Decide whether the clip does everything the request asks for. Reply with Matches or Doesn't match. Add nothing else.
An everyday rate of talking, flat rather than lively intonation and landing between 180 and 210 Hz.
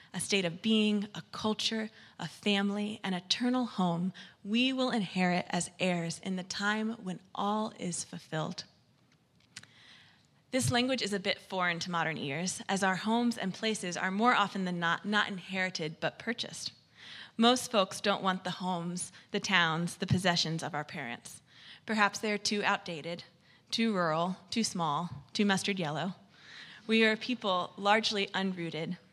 Doesn't match